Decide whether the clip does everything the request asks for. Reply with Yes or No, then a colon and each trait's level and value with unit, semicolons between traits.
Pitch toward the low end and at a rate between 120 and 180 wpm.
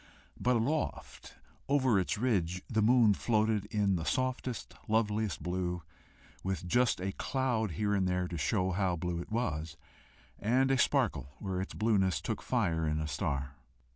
Yes: low, 100 Hz; average, 160 wpm